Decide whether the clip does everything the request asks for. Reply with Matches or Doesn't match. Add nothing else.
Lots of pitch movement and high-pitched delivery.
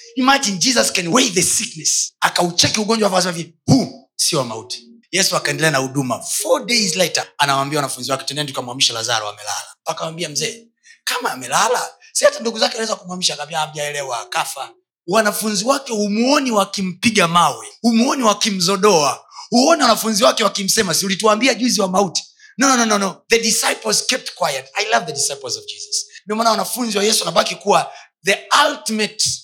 Matches